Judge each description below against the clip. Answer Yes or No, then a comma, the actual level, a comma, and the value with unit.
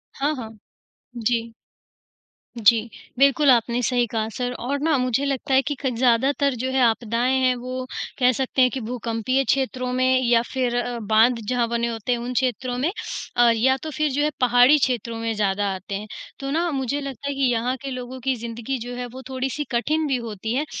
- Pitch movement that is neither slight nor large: No, narrow, 2.3 semitones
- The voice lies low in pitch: No, very high, 250 Hz